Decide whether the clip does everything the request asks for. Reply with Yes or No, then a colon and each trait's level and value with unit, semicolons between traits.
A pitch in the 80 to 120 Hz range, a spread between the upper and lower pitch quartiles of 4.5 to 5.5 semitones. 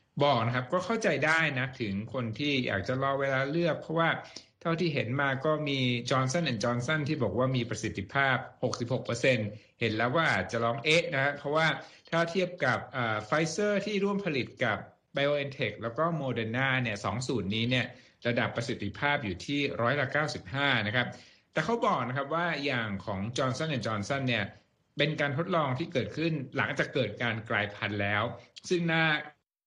No: low, 130 Hz; average, 4.8 semitones